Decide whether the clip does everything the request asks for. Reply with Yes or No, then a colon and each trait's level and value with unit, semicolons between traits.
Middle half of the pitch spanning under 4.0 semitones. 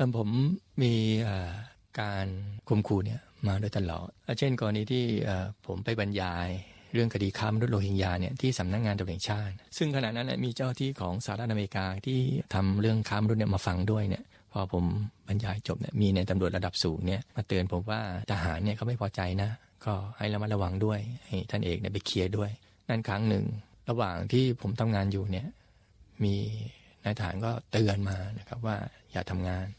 Yes: average, 2.7 semitones